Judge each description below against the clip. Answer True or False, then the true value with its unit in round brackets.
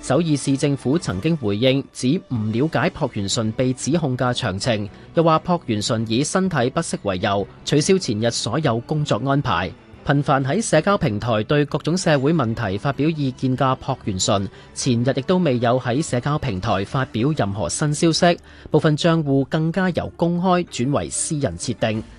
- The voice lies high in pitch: False (135 Hz)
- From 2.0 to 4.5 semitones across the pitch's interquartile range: False (5.0 semitones)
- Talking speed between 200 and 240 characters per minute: False (270 characters per minute)